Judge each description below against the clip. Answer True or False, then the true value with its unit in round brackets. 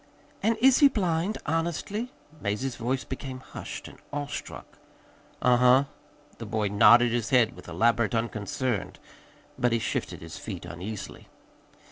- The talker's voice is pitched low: True (120 Hz)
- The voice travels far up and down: True (5.7 semitones)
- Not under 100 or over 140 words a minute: True (135 wpm)